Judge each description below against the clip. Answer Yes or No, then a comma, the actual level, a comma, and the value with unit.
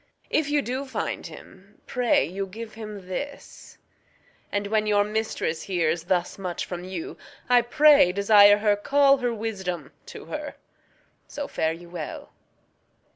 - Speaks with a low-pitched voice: No, high, 205 Hz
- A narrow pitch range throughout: No, average, 4.7 semitones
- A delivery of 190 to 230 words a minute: No, slow, 135 wpm